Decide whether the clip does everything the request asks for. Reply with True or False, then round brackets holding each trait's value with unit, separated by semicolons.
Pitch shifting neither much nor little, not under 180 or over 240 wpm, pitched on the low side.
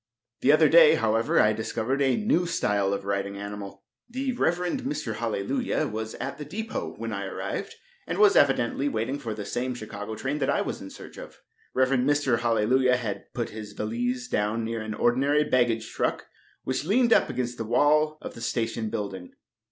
True (5.0 semitones; 185 wpm; 120 Hz)